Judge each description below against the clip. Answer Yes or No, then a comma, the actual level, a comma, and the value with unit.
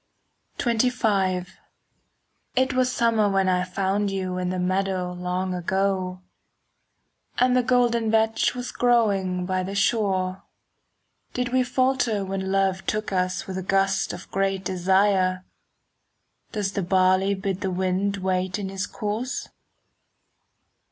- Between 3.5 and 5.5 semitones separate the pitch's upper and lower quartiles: No, average, 2.9 semitones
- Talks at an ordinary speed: No, slow, 130 wpm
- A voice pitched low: No, high, 195 Hz